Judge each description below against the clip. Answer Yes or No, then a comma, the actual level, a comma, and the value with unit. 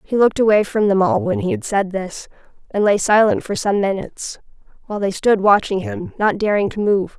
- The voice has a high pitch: Yes, high, 205 Hz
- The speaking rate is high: Yes, fast, 215 wpm